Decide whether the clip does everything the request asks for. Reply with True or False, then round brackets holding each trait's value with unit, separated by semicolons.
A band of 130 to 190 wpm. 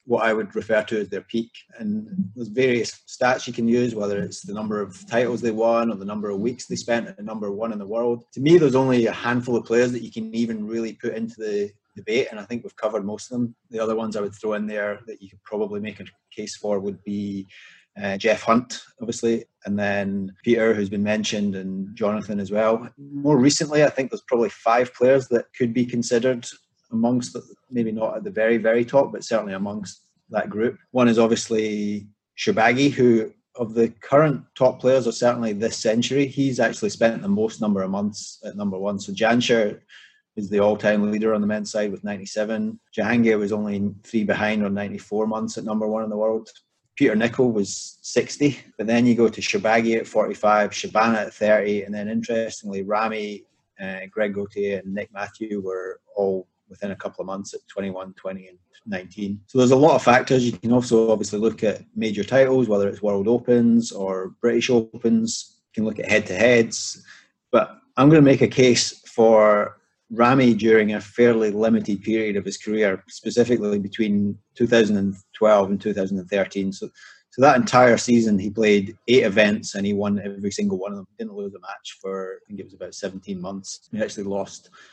False (205 wpm)